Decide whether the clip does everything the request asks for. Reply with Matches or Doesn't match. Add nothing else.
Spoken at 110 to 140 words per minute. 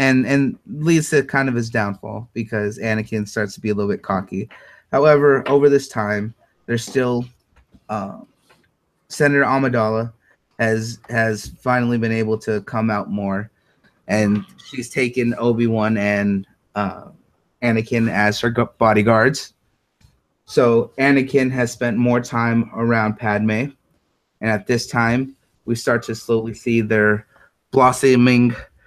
Matches